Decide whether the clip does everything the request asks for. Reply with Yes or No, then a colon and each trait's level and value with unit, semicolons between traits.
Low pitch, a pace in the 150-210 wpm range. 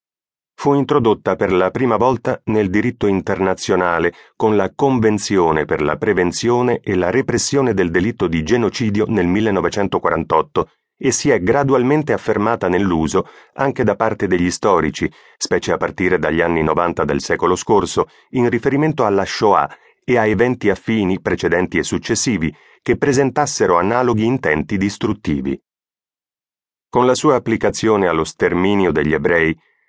No: low, 110 Hz; average, 135 wpm